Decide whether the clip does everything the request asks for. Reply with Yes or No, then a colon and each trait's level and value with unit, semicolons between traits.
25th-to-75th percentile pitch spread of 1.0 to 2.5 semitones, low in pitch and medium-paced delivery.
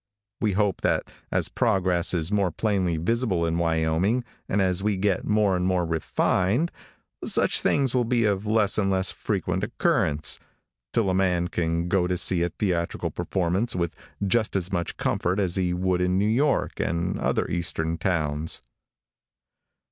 No: average, 3.2 semitones; very low, 95 Hz; average, 165 wpm